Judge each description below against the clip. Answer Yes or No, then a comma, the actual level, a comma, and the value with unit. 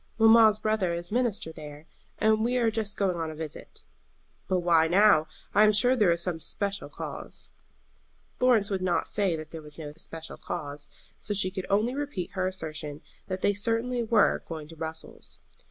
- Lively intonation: No, average, 5.0 semitones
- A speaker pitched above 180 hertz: Yes, high, 190 Hz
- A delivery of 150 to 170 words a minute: No, average, 185 wpm